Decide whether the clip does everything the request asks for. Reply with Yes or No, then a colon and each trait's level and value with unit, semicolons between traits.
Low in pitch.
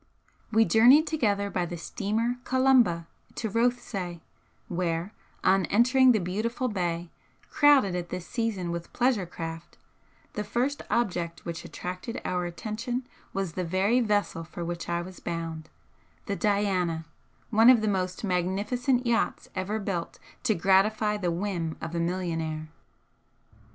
No: high, 195 Hz